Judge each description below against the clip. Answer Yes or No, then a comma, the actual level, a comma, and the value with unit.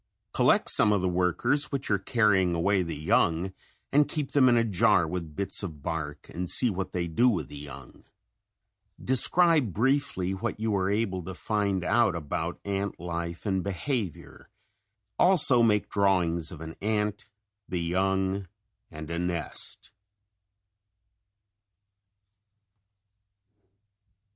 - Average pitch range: Yes, average, 4.2 semitones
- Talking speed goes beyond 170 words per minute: No, slow, 135 wpm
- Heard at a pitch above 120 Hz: No, very low, 95 Hz